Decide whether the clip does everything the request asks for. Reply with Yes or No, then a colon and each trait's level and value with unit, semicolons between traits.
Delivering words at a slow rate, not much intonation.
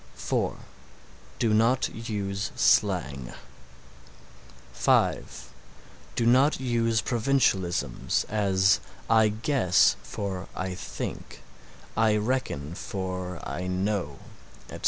No: slow, 90 wpm; average, 3.9 semitones